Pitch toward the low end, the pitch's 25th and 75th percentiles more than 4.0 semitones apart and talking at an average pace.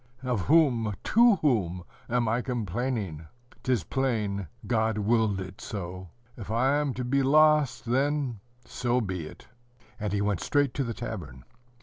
Yes: low, 115 Hz; average, 4.8 semitones; average, 155 wpm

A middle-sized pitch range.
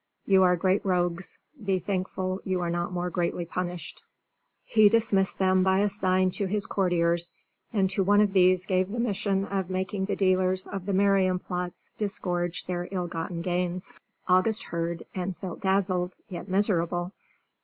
No: narrow, 1.6 semitones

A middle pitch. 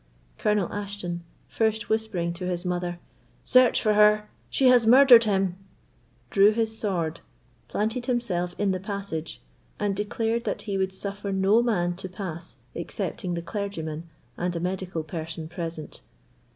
No: high, 195 Hz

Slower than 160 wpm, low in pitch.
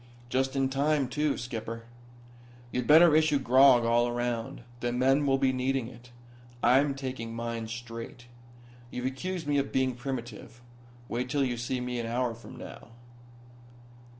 Yes: average, 150 wpm; low, 125 Hz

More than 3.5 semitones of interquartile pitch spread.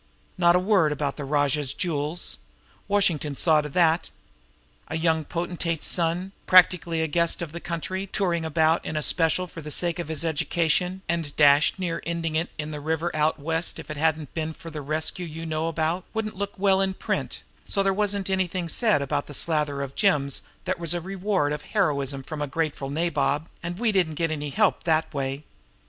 No: average, 3.0 semitones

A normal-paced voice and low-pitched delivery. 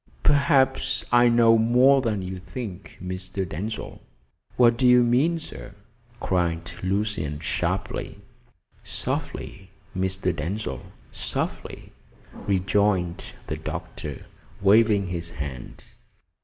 No: slow, 100 wpm; low, 100 Hz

